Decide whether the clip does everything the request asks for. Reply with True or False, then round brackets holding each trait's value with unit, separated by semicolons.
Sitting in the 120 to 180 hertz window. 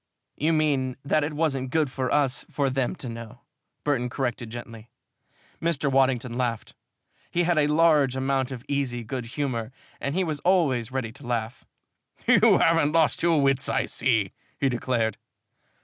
True (135 Hz)